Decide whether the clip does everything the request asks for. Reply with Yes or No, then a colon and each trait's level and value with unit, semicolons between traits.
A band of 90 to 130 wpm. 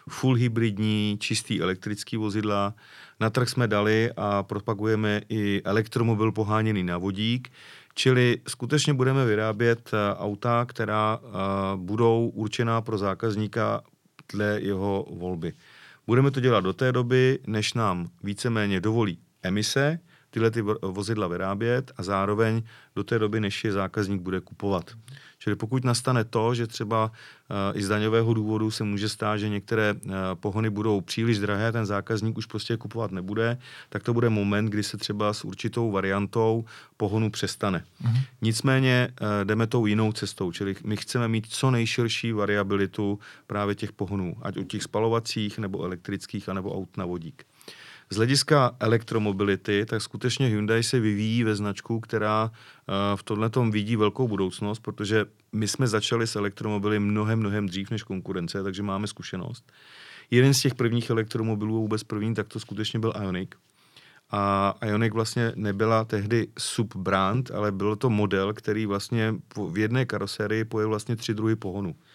No: average, 150 wpm